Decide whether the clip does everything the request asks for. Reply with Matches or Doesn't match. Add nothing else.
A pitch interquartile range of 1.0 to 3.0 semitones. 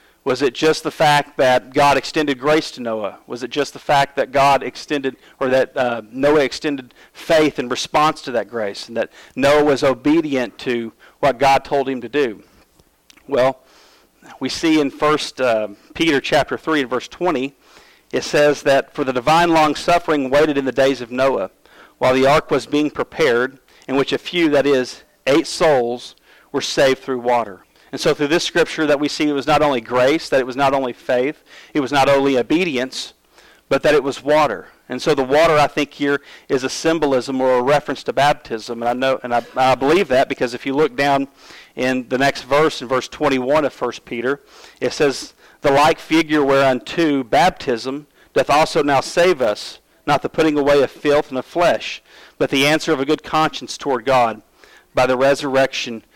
Matches